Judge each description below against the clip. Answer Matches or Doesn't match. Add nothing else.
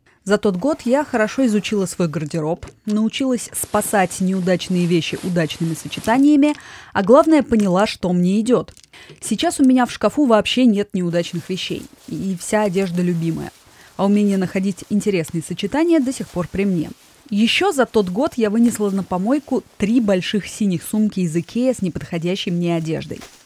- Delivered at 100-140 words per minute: Doesn't match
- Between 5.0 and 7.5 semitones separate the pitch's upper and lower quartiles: Doesn't match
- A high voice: Matches